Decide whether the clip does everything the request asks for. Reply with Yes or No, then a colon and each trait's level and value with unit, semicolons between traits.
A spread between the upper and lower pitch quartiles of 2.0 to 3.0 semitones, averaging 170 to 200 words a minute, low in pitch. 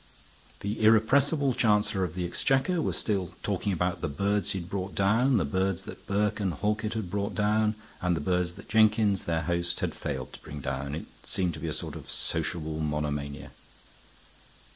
No: average, 4.5 semitones; average, 185 wpm; very low, 95 Hz